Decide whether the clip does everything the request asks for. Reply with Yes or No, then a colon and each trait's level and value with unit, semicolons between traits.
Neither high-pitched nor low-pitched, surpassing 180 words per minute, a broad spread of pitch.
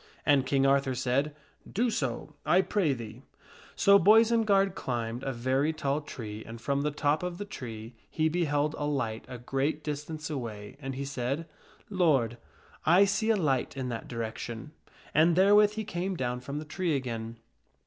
Yes: medium, 145 Hz; average, 190 wpm; wide, 5.7 semitones